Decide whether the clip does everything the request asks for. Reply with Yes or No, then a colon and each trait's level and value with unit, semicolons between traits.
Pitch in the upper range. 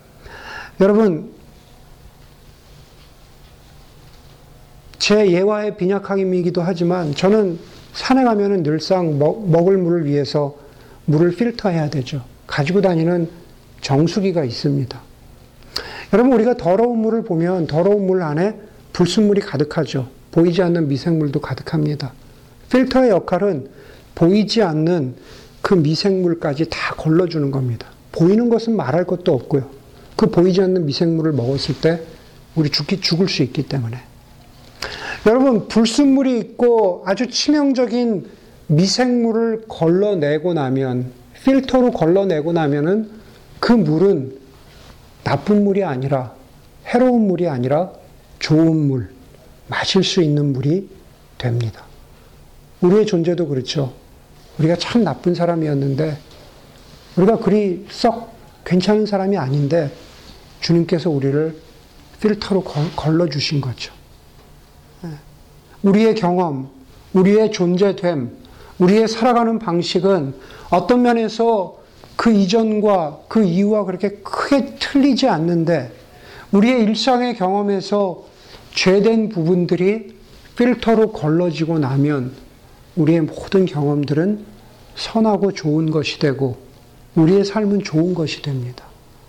No: medium, 175 Hz